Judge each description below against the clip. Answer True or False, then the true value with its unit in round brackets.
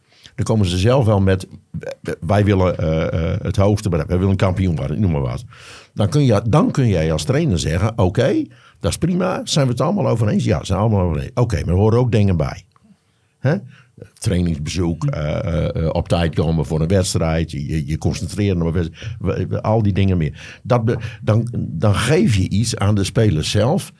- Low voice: True (100 Hz)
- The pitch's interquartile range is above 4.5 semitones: True (4.9 semitones)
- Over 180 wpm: True (200 wpm)